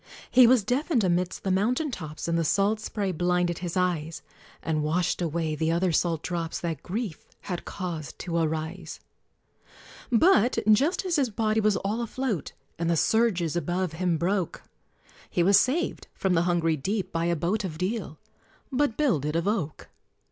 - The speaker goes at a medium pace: Yes, average, 170 wpm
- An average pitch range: Yes, average, 4.6 semitones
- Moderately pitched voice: Yes, medium, 180 Hz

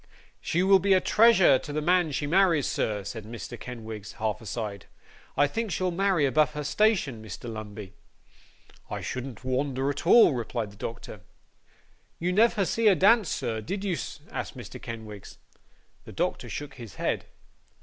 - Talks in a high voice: No, medium, 140 Hz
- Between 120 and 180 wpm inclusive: Yes, average, 165 wpm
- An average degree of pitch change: No, wide, 8.7 semitones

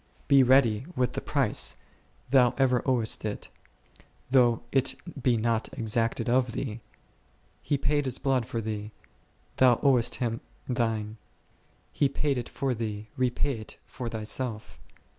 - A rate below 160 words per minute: Yes, average, 140 wpm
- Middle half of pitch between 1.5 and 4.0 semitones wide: Yes, average, 2.7 semitones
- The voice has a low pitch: Yes, low, 120 Hz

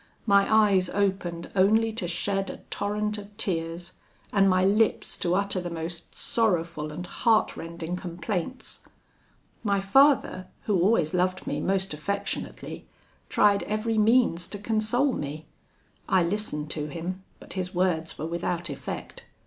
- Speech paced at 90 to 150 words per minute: Yes, average, 140 wpm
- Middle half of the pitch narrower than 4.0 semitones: Yes, average, 3.5 semitones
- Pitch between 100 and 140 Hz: No, high, 190 Hz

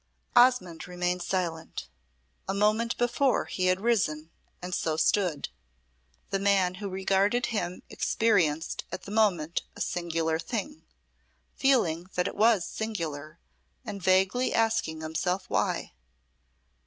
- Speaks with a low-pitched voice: No, medium, 185 Hz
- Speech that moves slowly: Yes, slow, 120 wpm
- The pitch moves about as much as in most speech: Yes, average, 4.4 semitones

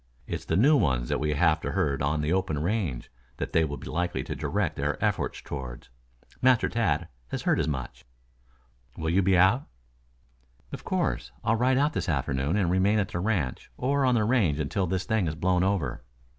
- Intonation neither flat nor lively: No, wide, 6.2 semitones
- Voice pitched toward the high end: No, very low, 90 Hz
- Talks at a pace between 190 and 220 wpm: Yes, average, 200 wpm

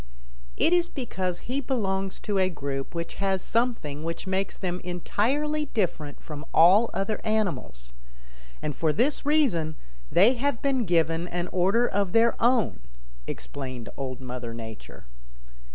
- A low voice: No, high, 190 Hz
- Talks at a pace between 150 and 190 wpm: No, average, 140 wpm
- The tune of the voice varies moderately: No, wide, 6.9 semitones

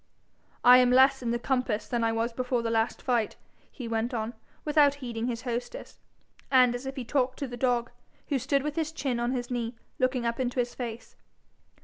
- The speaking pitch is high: Yes, high, 245 Hz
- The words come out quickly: Yes, fast, 210 wpm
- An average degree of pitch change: No, narrow, 2.0 semitones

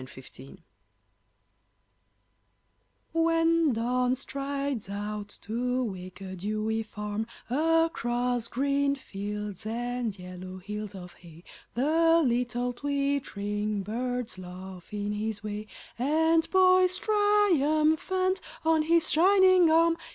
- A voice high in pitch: Yes, high, 245 Hz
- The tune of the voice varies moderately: No, wide, 7.5 semitones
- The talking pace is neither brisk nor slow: No, slow, 100 wpm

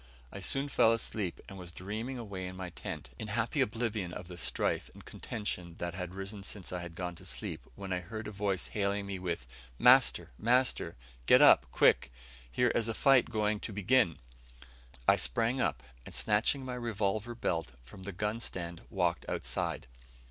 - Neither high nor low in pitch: No, low, 100 Hz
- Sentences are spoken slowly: No, average, 185 wpm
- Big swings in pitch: No, average, 4.0 semitones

